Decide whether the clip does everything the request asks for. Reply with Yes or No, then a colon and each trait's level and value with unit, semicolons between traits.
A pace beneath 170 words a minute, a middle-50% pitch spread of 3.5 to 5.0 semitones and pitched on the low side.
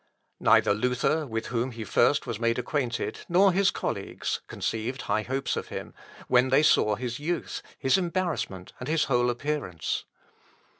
Yes: average, 150 wpm; average, 4.6 semitones; low, 125 Hz